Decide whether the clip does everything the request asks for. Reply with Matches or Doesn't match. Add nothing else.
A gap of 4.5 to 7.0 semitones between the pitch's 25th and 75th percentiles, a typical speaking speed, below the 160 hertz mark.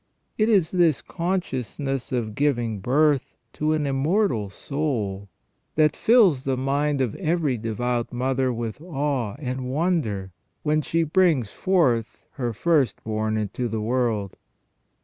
Doesn't match